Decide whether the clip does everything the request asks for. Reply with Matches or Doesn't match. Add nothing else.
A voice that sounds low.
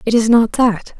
Doesn't match